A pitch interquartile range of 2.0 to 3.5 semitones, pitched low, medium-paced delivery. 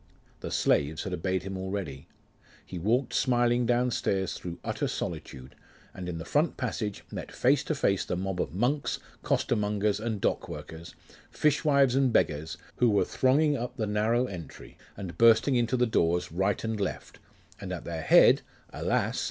No: average, 5.2 semitones; low, 105 Hz; average, 165 wpm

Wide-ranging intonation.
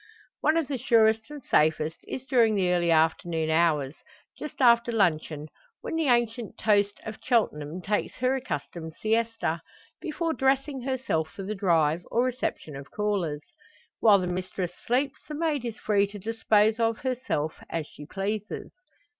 Yes: wide, 6.7 semitones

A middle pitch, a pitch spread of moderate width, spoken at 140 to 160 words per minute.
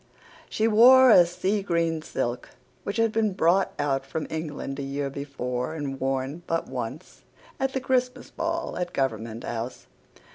No: medium, 160 Hz; wide, 7.8 semitones; average, 155 wpm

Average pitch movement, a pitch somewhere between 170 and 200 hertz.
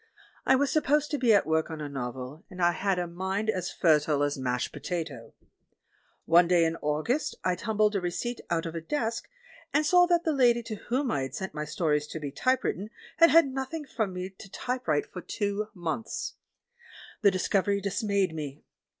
No: wide, 7.0 semitones; high, 190 Hz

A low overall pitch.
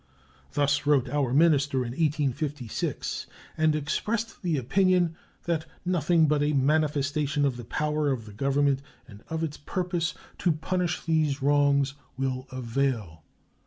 No: medium, 145 Hz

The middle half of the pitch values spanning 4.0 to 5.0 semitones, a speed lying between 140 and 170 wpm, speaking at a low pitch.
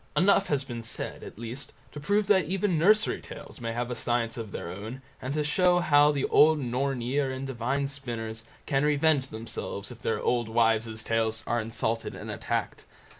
No: average, 4.5 semitones; average, 185 wpm; low, 130 Hz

